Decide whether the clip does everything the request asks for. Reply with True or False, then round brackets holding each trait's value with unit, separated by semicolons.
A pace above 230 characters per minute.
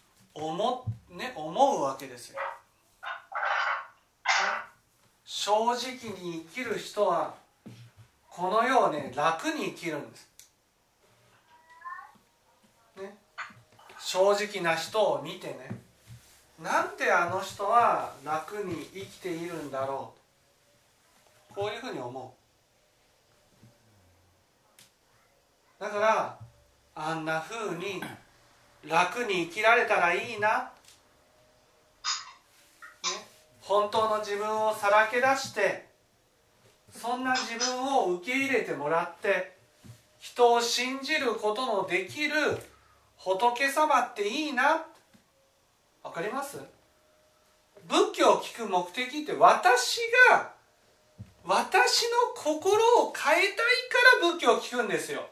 False (180 characters per minute)